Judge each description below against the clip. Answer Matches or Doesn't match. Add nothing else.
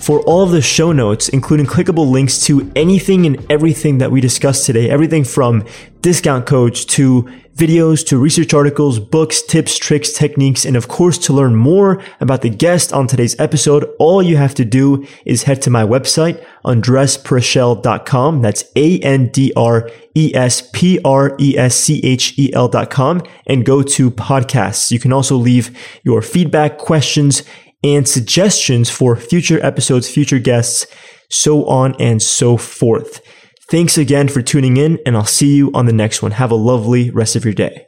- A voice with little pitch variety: Doesn't match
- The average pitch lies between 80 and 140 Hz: Matches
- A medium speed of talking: Matches